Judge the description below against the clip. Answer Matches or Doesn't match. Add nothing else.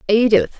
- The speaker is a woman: Matches